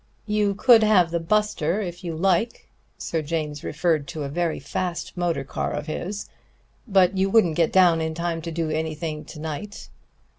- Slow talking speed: No, average, 180 wpm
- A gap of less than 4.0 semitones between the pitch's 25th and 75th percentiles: Yes, average, 3.4 semitones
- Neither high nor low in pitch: Yes, medium, 170 Hz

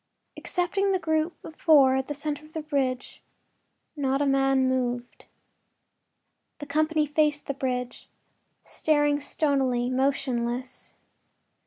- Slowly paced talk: Yes, slow, 120 wpm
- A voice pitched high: Yes, very high, 280 Hz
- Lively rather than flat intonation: No, average, 2.8 semitones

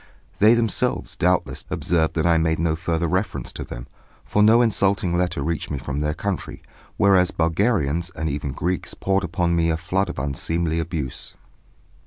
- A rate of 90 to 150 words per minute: No, average, 170 wpm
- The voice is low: Yes, very low, 85 Hz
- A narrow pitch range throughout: No, average, 3.3 semitones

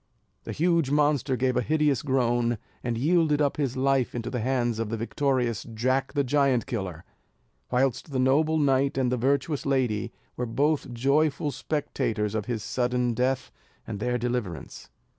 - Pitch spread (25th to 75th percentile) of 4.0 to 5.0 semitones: No, average, 2.8 semitones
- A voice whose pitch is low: Yes, low, 130 Hz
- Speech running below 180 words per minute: Yes, average, 160 wpm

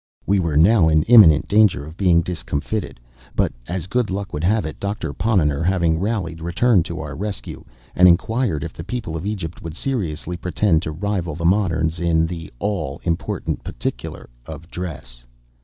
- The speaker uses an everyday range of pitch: Yes, average, 4.0 semitones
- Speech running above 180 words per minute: No, average, 175 wpm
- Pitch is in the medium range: No, very low, 85 Hz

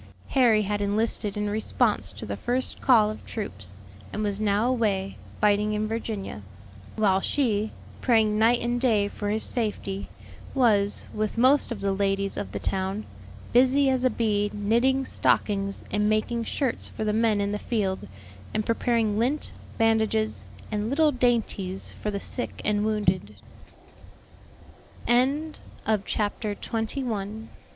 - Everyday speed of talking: Yes, average, 145 wpm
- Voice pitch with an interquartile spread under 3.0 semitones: Yes, narrow, 2.4 semitones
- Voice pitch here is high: Yes, high, 215 Hz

